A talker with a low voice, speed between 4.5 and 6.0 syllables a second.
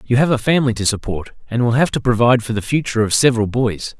No: low, 120 Hz; 6.9 syllables/s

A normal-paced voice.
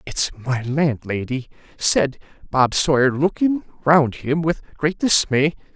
No: slow, 125 wpm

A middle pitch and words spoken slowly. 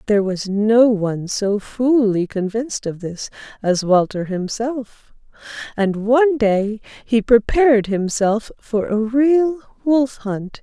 No: high, 225 Hz; slow, 130 wpm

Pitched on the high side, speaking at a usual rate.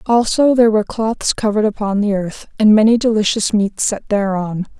Yes: high, 210 Hz; average, 175 wpm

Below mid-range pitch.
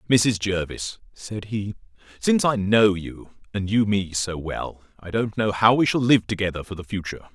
Yes: low, 100 Hz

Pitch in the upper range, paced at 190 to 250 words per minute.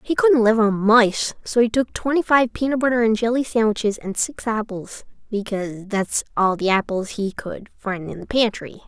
Yes: high, 220 Hz; average, 195 wpm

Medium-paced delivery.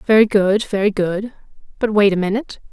Yes: average, 175 wpm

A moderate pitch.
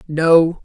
Yes: medium, 165 Hz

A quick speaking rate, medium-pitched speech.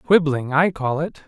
No: average, 190 wpm; medium, 155 Hz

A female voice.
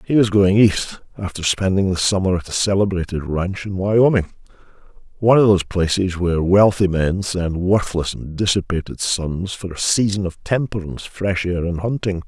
No: male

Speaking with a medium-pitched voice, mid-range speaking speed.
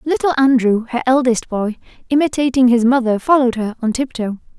No: very high, 250 Hz; average, 155 wpm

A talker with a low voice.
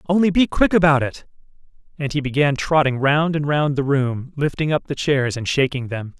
No: medium, 145 Hz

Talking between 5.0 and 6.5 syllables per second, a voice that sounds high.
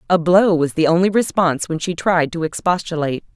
No: 5.8 syllables/s; medium, 170 Hz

